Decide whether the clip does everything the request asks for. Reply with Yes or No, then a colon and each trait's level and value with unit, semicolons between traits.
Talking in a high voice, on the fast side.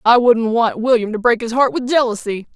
Yes: high, 230 Hz; fast, 235 wpm